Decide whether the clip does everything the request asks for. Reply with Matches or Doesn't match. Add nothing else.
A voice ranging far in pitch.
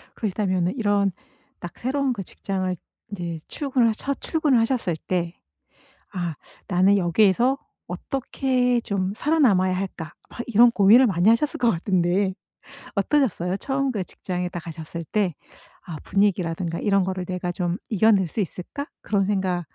Doesn't match